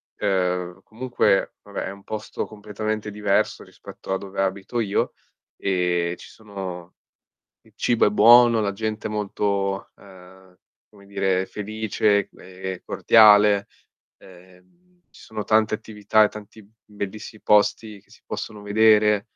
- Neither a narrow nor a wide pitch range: No, narrow, 2.0 semitones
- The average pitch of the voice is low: Yes, low, 100 Hz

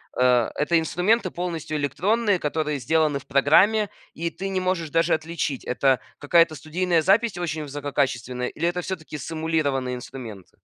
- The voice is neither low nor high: Yes, medium, 160 Hz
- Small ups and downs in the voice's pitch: No, average, 4.1 semitones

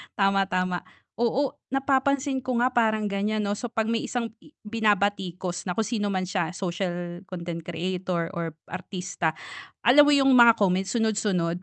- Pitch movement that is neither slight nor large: Yes, average, 4.4 semitones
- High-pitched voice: Yes, high, 200 Hz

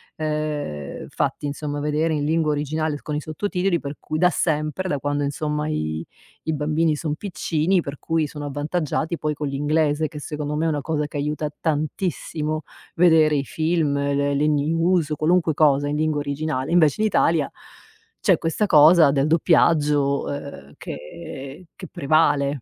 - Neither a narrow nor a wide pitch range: No, narrow, 1.8 semitones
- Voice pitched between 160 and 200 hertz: No, medium, 150 Hz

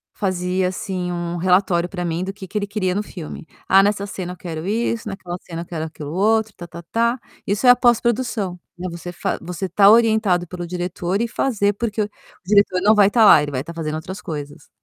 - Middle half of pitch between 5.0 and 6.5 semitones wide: No, average, 3.2 semitones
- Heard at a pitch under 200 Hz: Yes, medium, 185 Hz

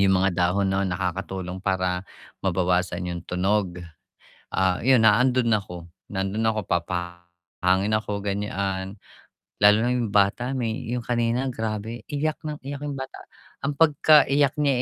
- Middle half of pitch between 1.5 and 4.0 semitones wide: No, average, 4.9 semitones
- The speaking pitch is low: Yes, low, 100 Hz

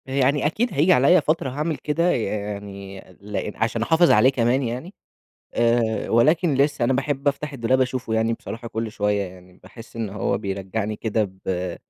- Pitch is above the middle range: No, low, 120 Hz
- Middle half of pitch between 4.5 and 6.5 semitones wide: Yes, average, 4.9 semitones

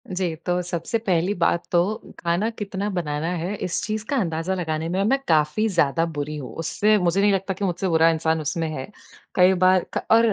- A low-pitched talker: No, medium, 175 Hz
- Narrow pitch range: No, average, 3.2 semitones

